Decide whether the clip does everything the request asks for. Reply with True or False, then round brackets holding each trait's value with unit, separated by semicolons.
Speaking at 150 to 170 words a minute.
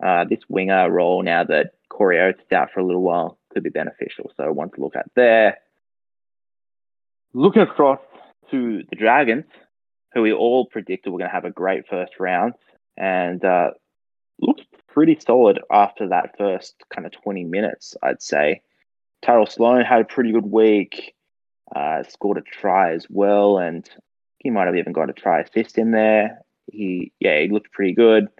False (180 wpm)